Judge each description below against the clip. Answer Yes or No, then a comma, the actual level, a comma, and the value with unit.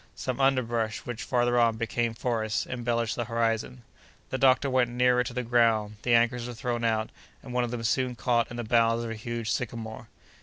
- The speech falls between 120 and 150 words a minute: No, average, 200 wpm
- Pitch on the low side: Yes, low, 120 Hz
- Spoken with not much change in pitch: Yes, narrow, 1.3 semitones